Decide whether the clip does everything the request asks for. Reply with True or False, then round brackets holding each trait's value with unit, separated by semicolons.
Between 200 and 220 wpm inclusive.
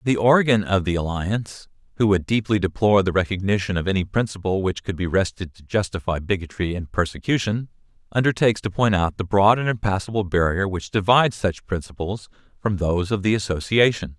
False (175 wpm)